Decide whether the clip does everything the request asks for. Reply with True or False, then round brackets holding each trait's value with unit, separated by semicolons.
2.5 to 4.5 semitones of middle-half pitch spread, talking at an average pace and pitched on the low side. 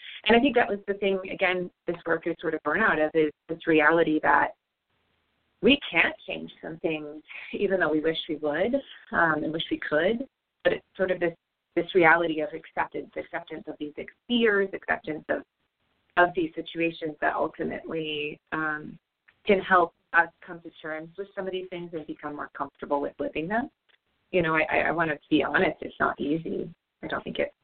False (3.3 semitones; 195 wpm; 165 Hz)